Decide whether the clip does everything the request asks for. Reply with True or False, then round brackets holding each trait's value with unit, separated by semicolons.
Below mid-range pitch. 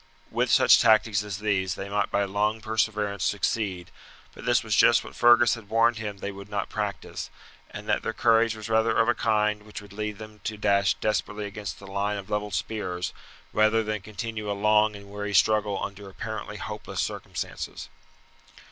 True (105 Hz)